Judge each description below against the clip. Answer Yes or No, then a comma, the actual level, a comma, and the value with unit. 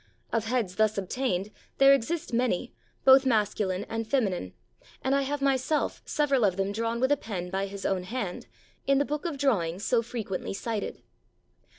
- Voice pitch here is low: No, high, 230 Hz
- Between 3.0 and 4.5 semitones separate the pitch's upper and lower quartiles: No, wide, 5.5 semitones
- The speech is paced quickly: No, average, 175 wpm